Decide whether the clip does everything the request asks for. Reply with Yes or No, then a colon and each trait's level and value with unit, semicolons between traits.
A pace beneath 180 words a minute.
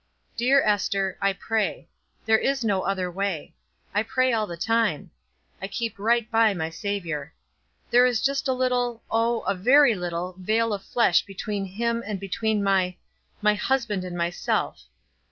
Yes: average, 160 wpm